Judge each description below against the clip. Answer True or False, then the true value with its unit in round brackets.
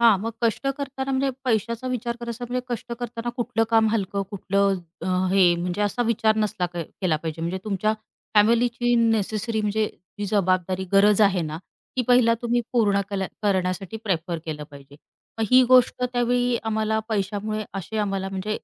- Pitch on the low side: False (215 Hz)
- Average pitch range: True (3.7 semitones)